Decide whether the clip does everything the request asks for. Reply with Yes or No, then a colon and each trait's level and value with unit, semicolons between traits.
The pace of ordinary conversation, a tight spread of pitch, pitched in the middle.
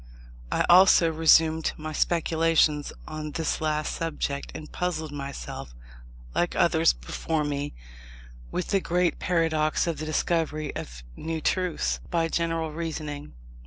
No: slow, 125 wpm; narrow, 1.6 semitones; medium, 160 Hz